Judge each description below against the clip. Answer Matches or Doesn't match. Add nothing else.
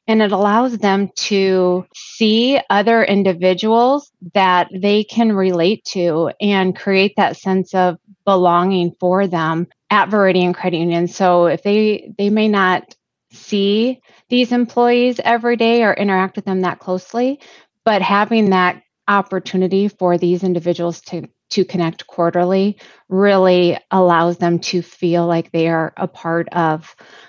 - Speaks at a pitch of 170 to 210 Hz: Matches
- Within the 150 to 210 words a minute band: Doesn't match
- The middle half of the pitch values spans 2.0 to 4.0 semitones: Matches